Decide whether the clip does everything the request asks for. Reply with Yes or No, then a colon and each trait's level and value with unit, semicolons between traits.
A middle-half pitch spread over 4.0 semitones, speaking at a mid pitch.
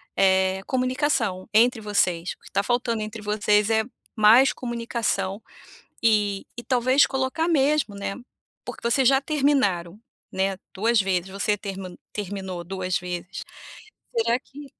No: average, 4.7 semitones; high, 210 Hz